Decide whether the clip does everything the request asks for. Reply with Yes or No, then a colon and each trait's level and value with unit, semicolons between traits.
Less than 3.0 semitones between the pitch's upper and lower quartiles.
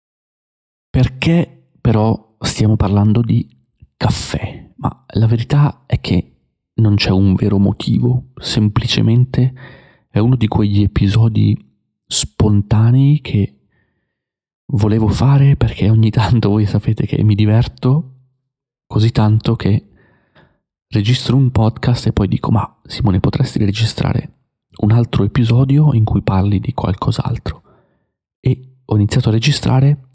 No: average, 3.8 semitones